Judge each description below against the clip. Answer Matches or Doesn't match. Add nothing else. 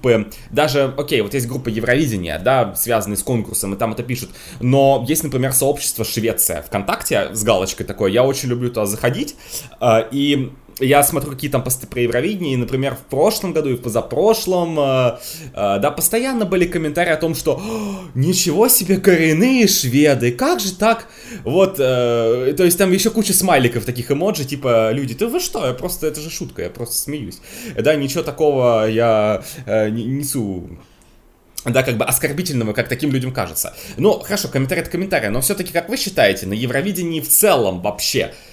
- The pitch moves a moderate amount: Doesn't match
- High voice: Doesn't match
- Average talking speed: Doesn't match